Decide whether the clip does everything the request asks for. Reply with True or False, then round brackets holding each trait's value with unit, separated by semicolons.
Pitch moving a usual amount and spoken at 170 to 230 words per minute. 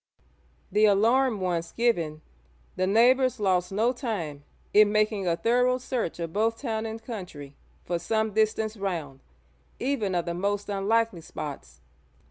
False (4.6 semitones; 140 wpm)